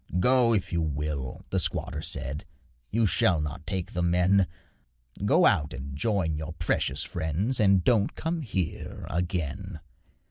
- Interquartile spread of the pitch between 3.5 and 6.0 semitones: Yes, average, 4.7 semitones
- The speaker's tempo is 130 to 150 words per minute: Yes, average, 145 wpm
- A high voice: No, very low, 90 Hz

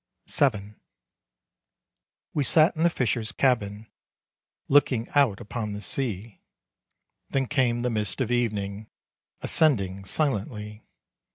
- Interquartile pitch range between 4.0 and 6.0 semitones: Yes, average, 4.5 semitones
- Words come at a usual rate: No, slow, 105 wpm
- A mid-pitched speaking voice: No, low, 115 Hz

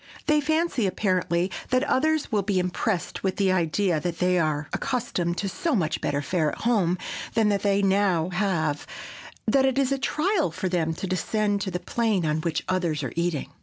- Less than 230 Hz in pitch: Yes, high, 190 Hz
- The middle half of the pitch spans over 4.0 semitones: Yes, average, 4.9 semitones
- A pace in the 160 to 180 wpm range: No, average, 195 wpm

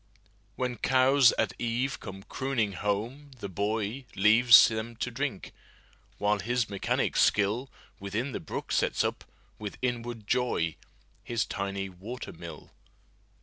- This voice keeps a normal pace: No, slow, 115 wpm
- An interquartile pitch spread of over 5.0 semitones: No, average, 3.8 semitones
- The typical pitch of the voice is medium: No, low, 115 Hz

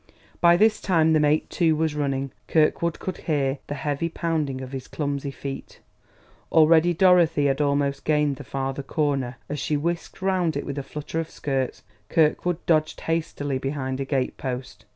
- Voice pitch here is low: No, medium, 150 Hz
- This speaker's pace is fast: No, average, 170 wpm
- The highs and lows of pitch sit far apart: No, average, 3.0 semitones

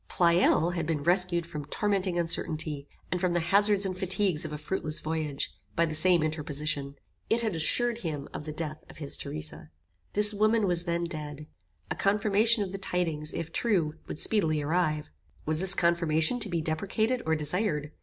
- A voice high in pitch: No, medium, 170 Hz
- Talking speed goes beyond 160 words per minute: Yes, average, 180 wpm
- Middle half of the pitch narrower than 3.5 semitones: No, average, 4.1 semitones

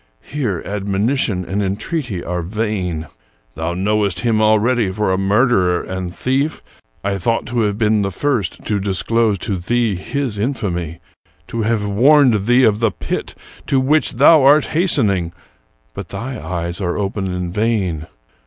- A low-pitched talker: Yes, low, 105 Hz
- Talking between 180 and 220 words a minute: No, average, 155 wpm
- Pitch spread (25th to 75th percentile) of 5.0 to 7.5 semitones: No, average, 4.4 semitones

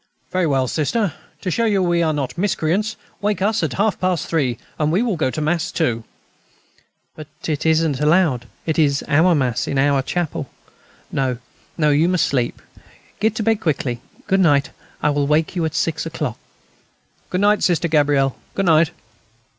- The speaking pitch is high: No, medium, 160 Hz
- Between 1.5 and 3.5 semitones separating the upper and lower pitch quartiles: No, average, 4.3 semitones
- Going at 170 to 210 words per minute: Yes, average, 180 wpm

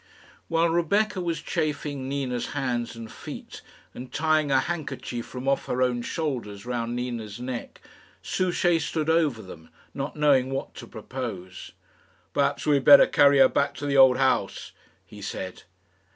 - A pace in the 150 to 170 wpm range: Yes, average, 155 wpm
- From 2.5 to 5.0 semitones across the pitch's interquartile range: Yes, average, 3.8 semitones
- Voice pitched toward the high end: No, low, 135 Hz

